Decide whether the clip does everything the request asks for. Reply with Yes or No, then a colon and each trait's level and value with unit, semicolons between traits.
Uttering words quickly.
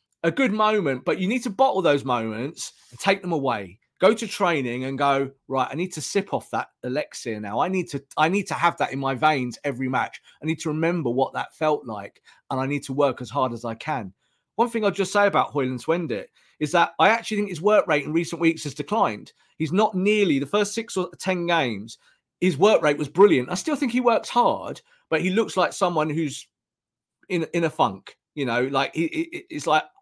Yes: fast, 235 wpm